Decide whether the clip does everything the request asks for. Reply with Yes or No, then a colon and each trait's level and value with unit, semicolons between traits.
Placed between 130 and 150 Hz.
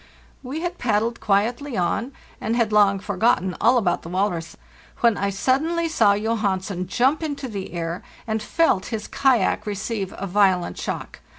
No: high, 210 Hz